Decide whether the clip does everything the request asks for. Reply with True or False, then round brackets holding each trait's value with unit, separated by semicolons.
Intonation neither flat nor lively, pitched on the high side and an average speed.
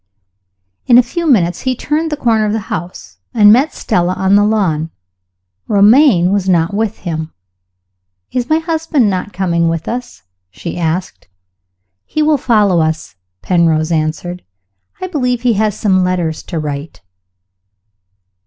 False (6.3 semitones; 200 Hz; 145 wpm)